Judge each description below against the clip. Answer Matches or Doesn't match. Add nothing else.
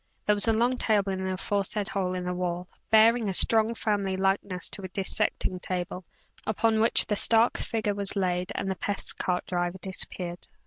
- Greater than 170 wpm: Matches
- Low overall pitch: Doesn't match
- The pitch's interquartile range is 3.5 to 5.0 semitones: Doesn't match